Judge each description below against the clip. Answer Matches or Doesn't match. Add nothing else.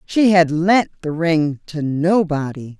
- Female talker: Matches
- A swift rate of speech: Doesn't match